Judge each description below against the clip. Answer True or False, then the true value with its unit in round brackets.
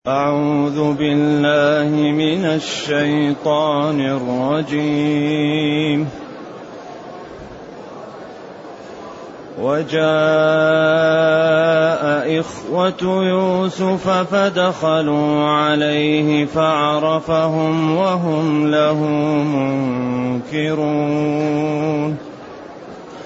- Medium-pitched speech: True (150 Hz)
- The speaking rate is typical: False (35 wpm)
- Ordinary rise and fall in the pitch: False (1.2 semitones)